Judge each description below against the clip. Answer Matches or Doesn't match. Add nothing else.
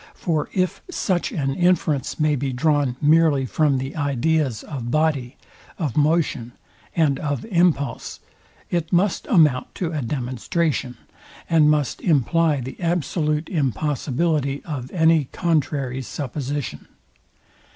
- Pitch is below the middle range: Doesn't match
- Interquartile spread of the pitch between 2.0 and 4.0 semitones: Matches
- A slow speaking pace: Matches